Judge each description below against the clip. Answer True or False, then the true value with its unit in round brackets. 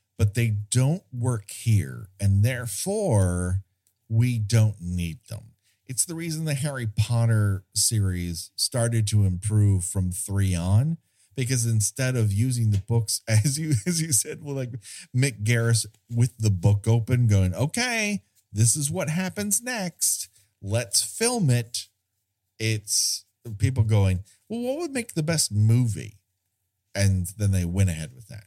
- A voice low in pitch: True (110 Hz)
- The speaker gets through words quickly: False (150 wpm)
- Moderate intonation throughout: True (4.2 semitones)